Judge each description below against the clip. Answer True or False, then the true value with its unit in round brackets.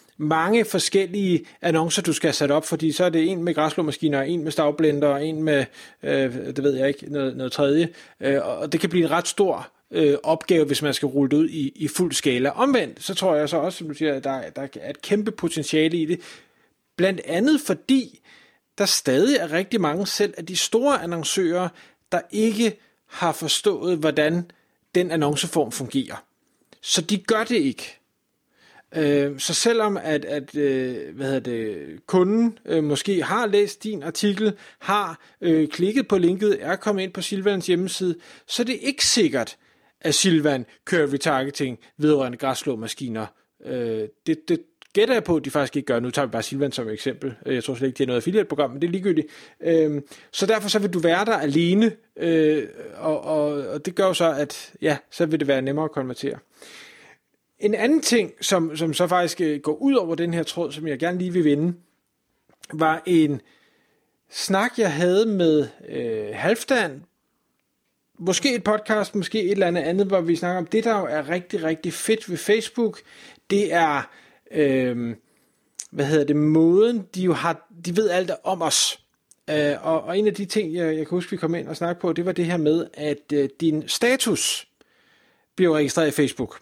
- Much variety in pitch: False (5.0 semitones)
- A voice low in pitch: False (165 Hz)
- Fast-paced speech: False (190 wpm)